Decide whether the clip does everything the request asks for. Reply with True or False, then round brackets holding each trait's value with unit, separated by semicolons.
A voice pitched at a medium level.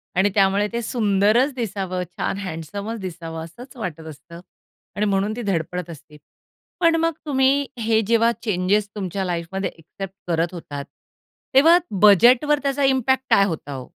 False (200 Hz)